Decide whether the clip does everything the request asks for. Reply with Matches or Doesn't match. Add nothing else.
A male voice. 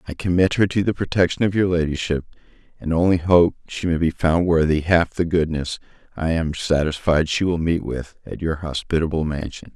Matches